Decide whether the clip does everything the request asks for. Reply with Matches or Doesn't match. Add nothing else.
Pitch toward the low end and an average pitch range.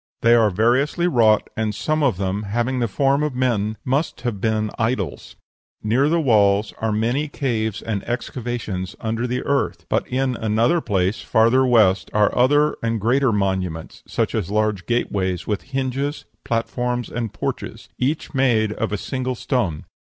Matches